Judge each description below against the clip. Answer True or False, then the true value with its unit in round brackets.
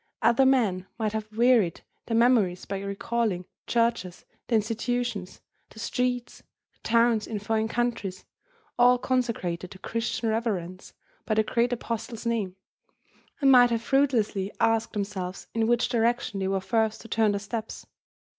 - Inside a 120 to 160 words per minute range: True (150 wpm)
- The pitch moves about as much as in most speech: True (3.0 semitones)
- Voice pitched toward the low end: False (225 Hz)